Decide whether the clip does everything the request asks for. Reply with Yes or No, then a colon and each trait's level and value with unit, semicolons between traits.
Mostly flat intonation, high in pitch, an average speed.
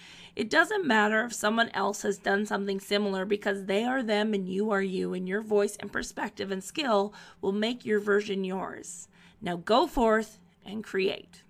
Yes: narrow, 2.0 semitones; high, 205 Hz; average, 185 wpm